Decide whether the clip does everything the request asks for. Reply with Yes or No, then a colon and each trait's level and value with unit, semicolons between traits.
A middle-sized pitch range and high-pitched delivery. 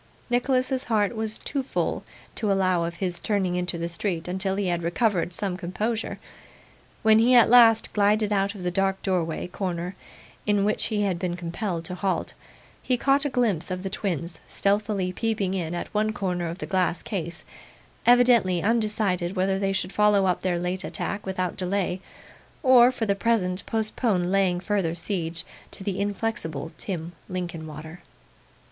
Yes: average, 3.2 semitones; high, 195 Hz